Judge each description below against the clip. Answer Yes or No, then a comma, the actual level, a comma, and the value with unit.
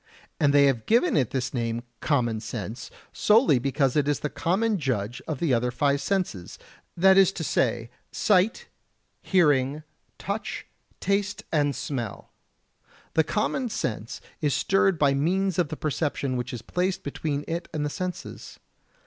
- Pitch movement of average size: No, wide, 6.2 semitones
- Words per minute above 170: No, average, 155 wpm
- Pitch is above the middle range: No, medium, 145 Hz